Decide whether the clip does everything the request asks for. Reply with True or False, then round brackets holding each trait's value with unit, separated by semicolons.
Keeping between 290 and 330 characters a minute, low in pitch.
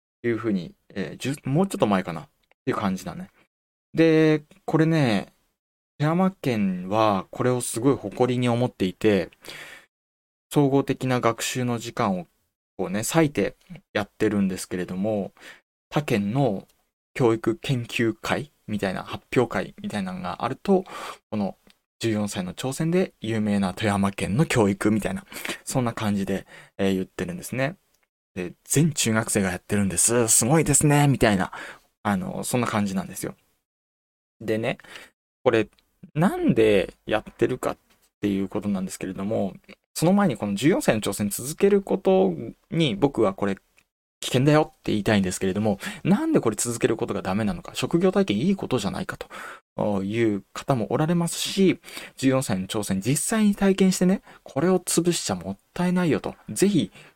True (315 characters per minute; 120 Hz)